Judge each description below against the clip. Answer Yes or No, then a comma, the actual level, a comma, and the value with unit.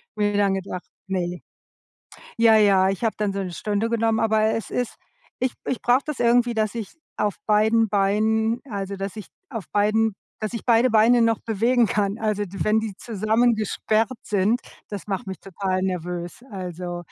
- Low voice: No, high, 215 Hz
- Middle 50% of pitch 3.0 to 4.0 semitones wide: No, narrow, 2.6 semitones